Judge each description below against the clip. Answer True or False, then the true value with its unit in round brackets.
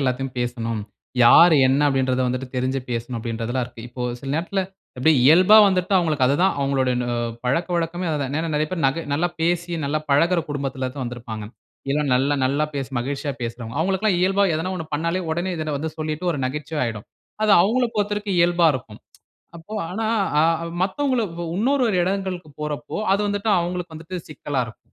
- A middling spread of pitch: False (5.7 semitones)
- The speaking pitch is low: False (155 Hz)